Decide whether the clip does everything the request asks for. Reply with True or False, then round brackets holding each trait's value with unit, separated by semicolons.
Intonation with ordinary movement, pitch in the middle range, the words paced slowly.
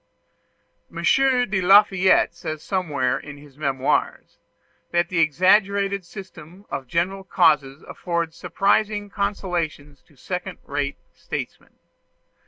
True (4.7 semitones; 175 Hz; 105 wpm)